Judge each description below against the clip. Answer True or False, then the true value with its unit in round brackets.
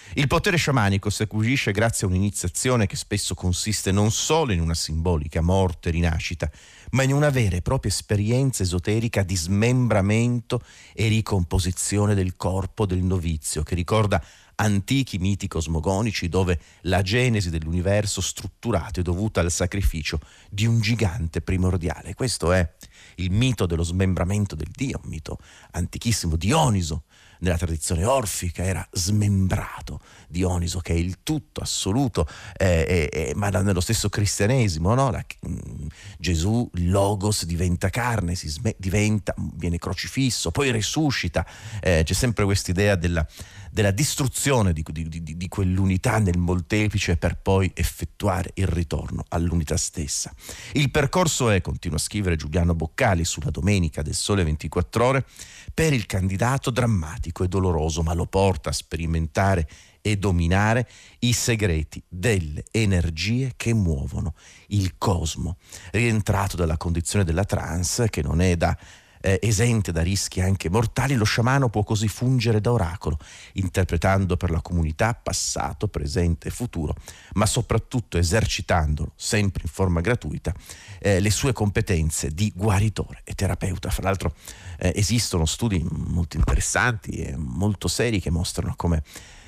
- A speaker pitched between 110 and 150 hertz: False (95 Hz)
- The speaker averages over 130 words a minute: True (140 wpm)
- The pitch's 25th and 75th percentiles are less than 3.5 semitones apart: False (3.8 semitones)